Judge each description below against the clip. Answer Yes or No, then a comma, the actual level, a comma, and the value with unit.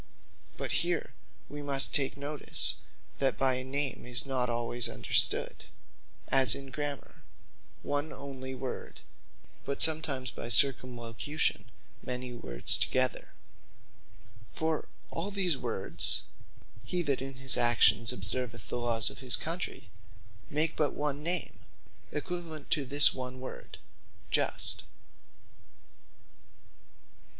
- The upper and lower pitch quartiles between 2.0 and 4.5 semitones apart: Yes, average, 2.9 semitones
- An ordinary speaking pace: No, slow, 115 wpm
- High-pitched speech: No, low, 135 Hz